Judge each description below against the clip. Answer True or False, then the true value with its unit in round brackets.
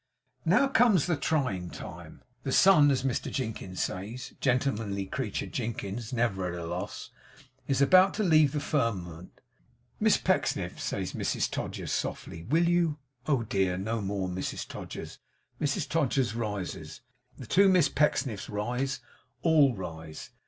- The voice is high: False (125 Hz)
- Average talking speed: True (145 wpm)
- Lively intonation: True (7.1 semitones)